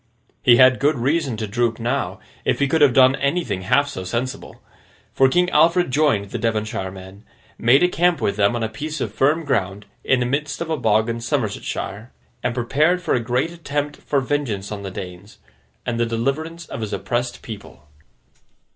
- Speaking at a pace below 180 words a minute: No, average, 190 wpm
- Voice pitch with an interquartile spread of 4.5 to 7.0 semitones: Yes, average, 5.1 semitones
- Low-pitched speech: Yes, low, 125 Hz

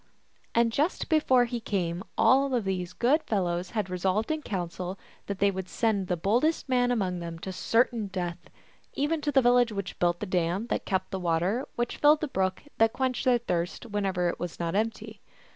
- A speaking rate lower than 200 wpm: No, fast, 205 wpm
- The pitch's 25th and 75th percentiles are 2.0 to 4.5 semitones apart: No, average, 5.2 semitones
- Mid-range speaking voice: No, high, 200 Hz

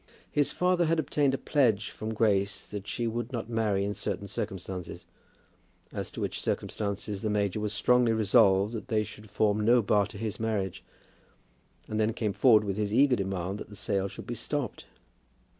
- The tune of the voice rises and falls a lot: No, average, 2.7 semitones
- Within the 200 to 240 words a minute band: No, average, 185 wpm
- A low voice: Yes, low, 105 Hz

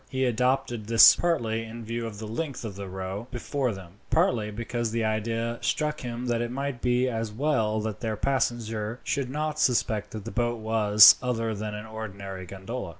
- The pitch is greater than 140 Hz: No, low, 115 Hz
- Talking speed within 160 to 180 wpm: No, average, 190 wpm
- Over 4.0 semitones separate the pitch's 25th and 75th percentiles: No, narrow, 2.5 semitones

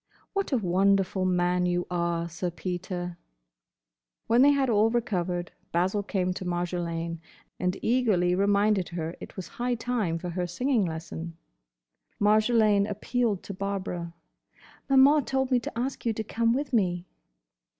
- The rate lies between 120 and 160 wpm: Yes, average, 145 wpm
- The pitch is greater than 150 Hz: Yes, high, 190 Hz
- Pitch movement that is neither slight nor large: Yes, average, 4.5 semitones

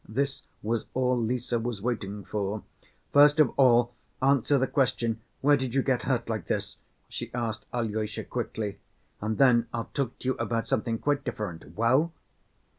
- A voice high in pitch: No, low, 120 Hz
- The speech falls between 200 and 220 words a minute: No, average, 165 wpm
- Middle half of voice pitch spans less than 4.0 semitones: Yes, average, 3.2 semitones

